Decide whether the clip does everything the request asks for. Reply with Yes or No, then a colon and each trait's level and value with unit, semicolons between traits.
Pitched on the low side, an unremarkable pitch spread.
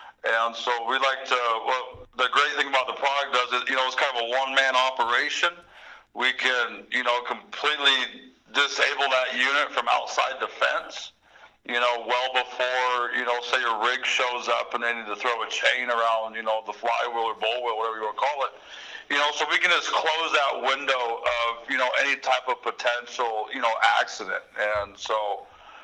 No: low, 125 Hz; narrow, 1.7 semitones